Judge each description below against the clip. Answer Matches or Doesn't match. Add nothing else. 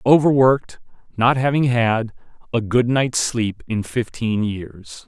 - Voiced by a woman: Doesn't match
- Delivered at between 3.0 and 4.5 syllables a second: Matches